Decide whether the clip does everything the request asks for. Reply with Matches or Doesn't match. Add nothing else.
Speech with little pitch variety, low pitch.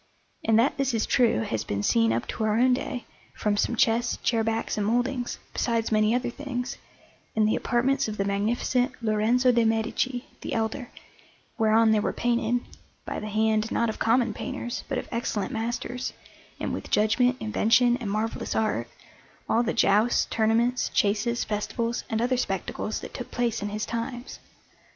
Doesn't match